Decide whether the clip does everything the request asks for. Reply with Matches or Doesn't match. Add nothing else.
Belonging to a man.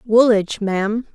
Doesn't match